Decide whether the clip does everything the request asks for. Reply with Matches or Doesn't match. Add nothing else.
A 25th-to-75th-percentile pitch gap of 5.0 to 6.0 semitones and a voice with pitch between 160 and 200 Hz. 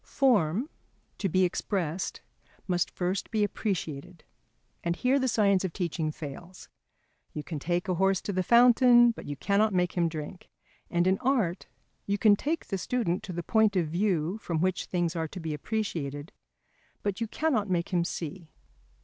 Doesn't match